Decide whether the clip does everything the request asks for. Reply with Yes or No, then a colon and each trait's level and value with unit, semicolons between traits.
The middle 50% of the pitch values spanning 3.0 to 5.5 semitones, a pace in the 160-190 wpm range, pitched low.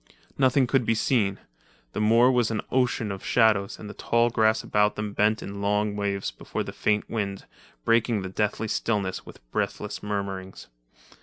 No: narrow, 2.4 semitones; average, 170 wpm; low, 105 Hz